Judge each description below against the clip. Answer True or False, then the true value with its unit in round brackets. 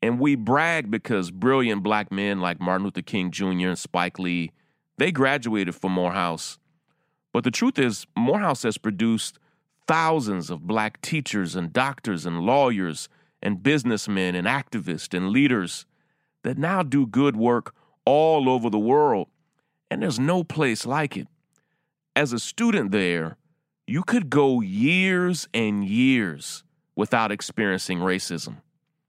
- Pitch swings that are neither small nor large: False (8.5 semitones)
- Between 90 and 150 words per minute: True (140 wpm)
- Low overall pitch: True (130 Hz)